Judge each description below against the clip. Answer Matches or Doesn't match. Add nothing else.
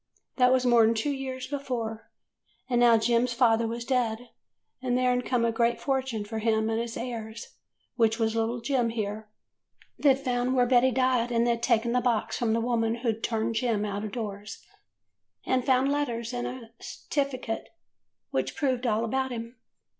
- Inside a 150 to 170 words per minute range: Doesn't match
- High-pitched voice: Matches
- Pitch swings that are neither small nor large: Doesn't match